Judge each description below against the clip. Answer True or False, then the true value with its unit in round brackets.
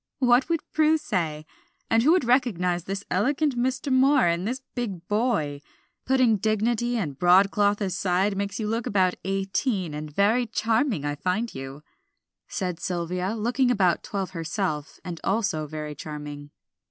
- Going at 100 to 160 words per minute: True (150 wpm)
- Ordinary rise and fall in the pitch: False (5.8 semitones)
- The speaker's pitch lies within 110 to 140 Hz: False (200 Hz)